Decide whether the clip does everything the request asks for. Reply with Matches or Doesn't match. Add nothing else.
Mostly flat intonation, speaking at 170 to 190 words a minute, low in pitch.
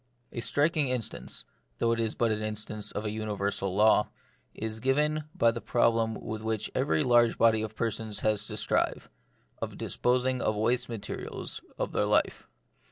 Matches